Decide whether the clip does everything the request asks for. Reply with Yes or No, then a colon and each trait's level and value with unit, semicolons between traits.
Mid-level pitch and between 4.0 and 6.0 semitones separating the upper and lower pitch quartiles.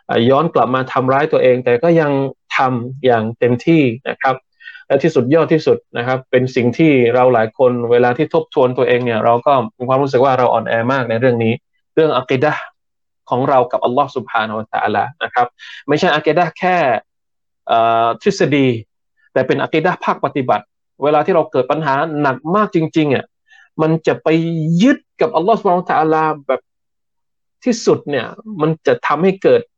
Yes: medium, 145 Hz; average, 4.8 semitones